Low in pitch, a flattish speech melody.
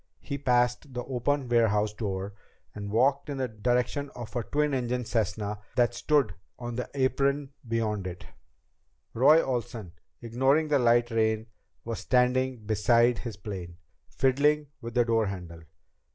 No: low, 120 Hz; average, 3.4 semitones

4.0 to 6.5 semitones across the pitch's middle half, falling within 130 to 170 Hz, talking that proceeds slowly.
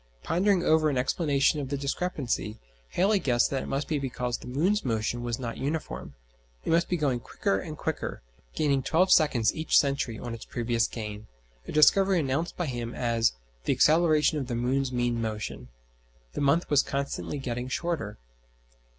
No: average, 4.7 semitones; low, 135 Hz; average, 175 wpm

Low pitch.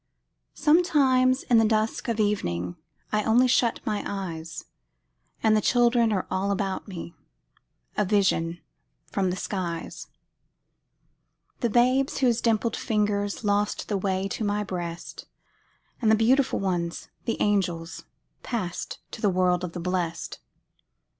No: high, 205 Hz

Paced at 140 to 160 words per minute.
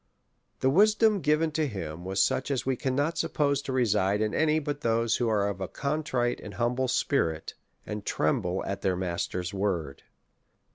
No: average, 175 wpm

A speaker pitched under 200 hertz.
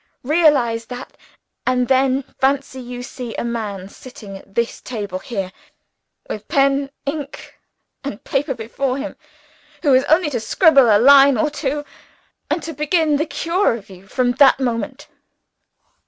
No: very high, 260 Hz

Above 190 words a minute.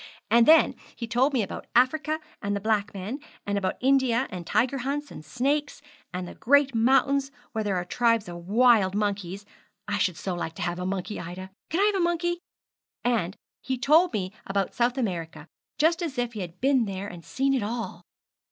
Yes: average, 200 wpm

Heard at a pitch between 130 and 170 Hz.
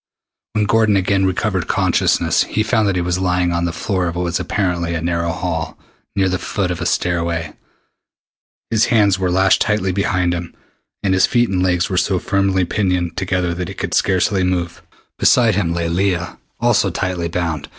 No: very low, 90 Hz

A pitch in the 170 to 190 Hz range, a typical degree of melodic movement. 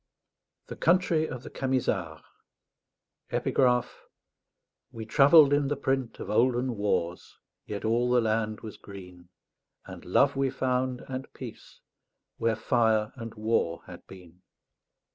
No: low, 115 Hz; average, 3.7 semitones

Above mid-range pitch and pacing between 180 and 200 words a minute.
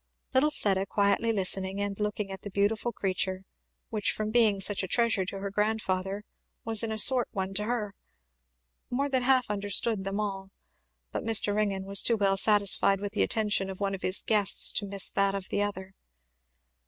Yes: high, 205 Hz; average, 190 wpm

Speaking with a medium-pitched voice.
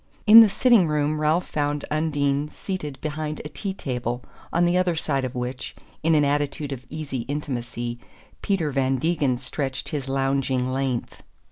Yes: medium, 145 Hz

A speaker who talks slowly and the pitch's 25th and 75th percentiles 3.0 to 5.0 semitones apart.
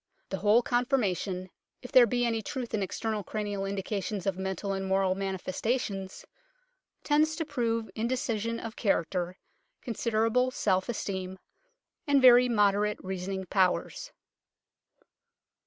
Yes: slow, 125 wpm; average, 3.8 semitones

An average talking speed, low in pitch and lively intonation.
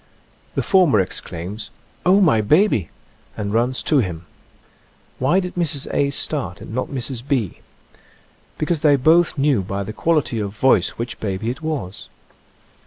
Yes: average, 160 wpm; low, 130 Hz; wide, 6.9 semitones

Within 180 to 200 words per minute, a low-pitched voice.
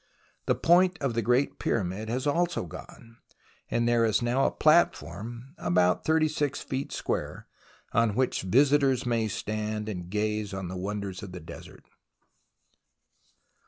No: average, 140 wpm; low, 115 Hz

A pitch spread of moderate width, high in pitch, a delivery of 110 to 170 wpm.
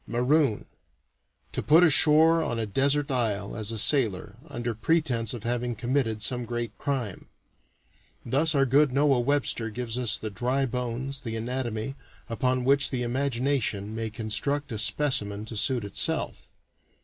No: average, 3.7 semitones; low, 125 Hz; average, 150 wpm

